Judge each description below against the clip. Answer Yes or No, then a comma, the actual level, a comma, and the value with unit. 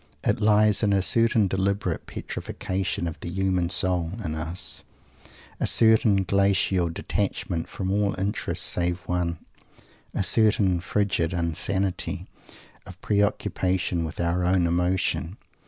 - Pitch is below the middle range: Yes, very low, 95 Hz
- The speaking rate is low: Yes, slow, 120 wpm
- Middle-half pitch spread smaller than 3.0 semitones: Yes, narrow, 2.5 semitones